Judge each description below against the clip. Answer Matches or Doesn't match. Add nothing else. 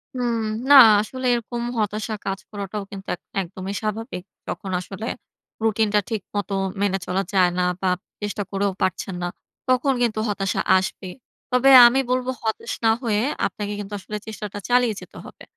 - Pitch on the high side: Matches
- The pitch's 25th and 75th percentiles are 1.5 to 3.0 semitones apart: Matches